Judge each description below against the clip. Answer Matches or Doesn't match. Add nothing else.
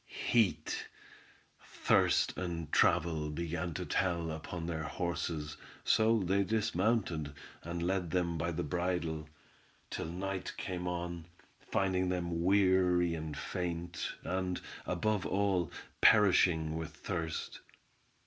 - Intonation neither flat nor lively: Doesn't match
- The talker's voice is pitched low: Matches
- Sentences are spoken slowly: Matches